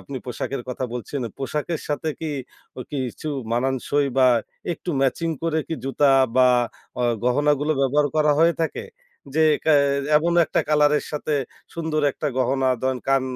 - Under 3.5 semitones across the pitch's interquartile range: Yes, average, 2.9 semitones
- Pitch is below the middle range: No, medium, 145 Hz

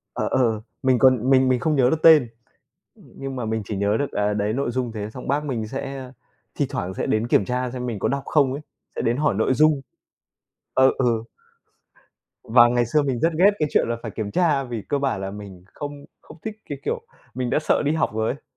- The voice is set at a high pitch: No, low, 125 Hz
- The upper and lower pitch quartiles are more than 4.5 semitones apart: No, average, 4.0 semitones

